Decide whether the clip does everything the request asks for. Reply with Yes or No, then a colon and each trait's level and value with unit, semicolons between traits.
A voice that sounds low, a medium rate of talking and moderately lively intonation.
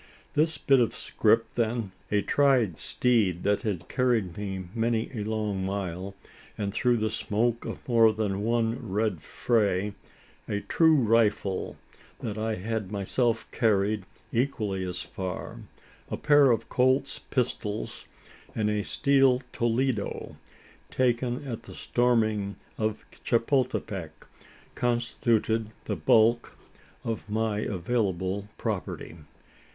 No: low, 110 Hz; slow, 120 wpm; average, 3.0 semitones